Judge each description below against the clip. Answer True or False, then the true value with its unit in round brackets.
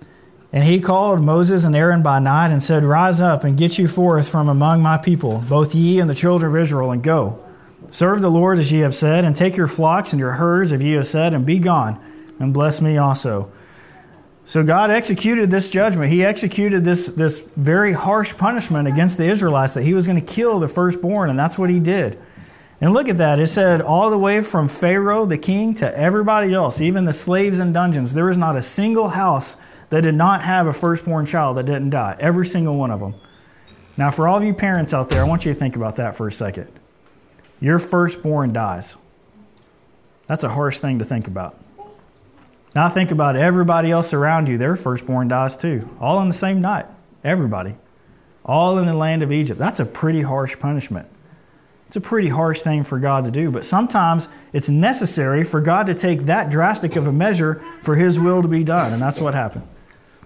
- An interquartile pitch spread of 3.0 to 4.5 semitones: True (4.0 semitones)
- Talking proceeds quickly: True (210 wpm)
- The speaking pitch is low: False (160 Hz)